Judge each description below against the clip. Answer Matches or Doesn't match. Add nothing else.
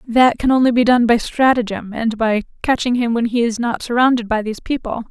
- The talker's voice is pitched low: Doesn't match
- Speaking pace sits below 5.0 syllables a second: Doesn't match